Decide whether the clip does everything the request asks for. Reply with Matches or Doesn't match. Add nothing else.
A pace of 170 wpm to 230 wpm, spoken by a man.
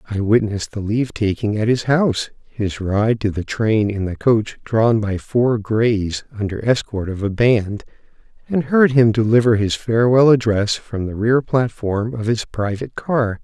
Matches